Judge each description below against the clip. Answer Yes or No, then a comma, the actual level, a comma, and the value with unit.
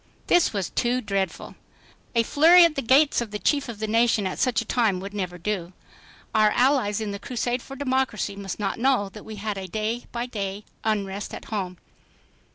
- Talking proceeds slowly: No, average, 200 wpm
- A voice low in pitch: No, high, 215 Hz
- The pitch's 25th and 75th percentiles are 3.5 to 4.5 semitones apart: Yes, average, 3.9 semitones